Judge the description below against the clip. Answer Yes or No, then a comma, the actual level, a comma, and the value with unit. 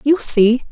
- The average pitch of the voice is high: Yes, very high, 255 Hz